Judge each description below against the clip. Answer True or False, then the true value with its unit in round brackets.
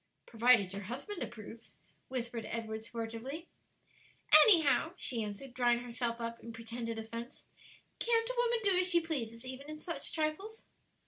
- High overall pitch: True (245 Hz)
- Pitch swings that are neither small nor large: False (5.8 semitones)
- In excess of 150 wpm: False (145 wpm)